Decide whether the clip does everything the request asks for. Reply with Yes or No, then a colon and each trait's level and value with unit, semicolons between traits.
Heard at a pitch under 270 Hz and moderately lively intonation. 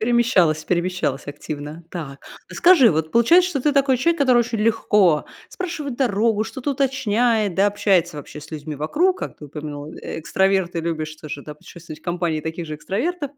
No: high, 190 Hz; wide, 7.9 semitones